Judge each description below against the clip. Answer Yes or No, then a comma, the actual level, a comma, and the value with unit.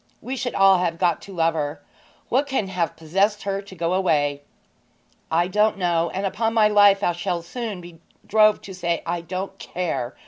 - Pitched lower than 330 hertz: Yes, medium, 185 Hz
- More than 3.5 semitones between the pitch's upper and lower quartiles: No, average, 3.2 semitones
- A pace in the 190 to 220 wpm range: Yes, average, 195 wpm